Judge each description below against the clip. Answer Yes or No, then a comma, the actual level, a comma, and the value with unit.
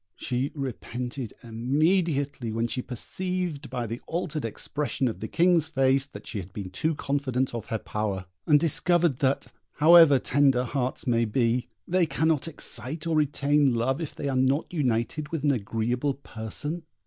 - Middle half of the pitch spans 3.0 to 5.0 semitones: Yes, average, 4.3 semitones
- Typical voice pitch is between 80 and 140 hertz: Yes, low, 135 Hz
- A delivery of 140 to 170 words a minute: Yes, average, 160 wpm